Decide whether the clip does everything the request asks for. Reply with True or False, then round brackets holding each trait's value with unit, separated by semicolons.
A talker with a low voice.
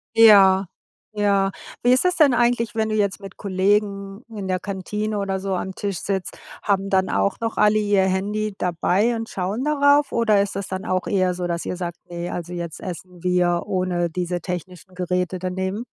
False (195 Hz)